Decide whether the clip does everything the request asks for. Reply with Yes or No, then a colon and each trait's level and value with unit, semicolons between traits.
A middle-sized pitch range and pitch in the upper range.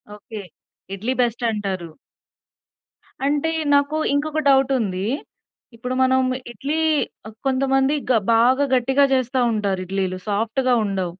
Yes: average, 4.7 semitones; high, 245 Hz